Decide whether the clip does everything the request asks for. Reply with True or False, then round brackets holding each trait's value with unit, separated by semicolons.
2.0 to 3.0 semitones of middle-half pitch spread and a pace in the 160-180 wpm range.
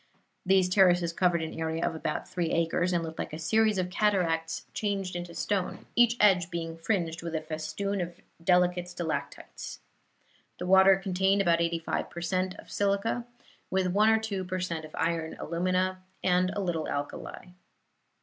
True (2.4 semitones; 170 wpm)